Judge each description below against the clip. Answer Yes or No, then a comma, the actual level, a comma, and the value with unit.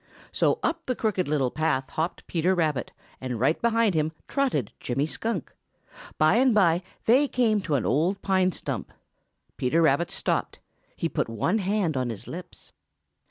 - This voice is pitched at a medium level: Yes, medium, 170 Hz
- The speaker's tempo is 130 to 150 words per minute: No, average, 160 wpm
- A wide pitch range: Yes, wide, 7.0 semitones